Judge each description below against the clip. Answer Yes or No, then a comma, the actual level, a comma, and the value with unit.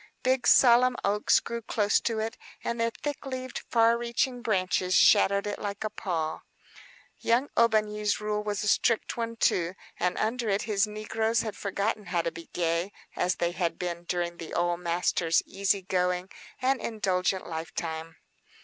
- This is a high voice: Yes, high, 205 Hz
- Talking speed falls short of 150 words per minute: No, average, 165 wpm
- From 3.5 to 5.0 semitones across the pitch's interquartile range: Yes, average, 4.3 semitones